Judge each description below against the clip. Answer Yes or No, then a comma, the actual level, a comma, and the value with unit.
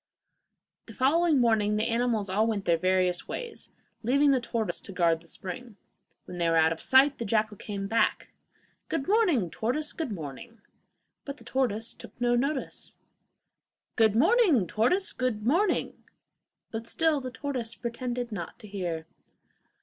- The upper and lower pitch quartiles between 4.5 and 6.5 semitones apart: Yes, average, 5.2 semitones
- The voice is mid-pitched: No, high, 230 Hz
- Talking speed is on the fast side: No, average, 155 wpm